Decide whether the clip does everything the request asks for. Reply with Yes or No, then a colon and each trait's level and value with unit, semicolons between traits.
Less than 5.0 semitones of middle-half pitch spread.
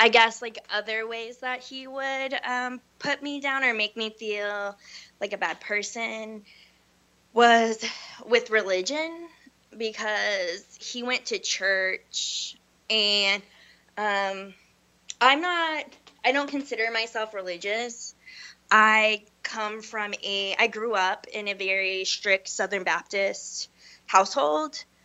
Yes: average, 3.8 semitones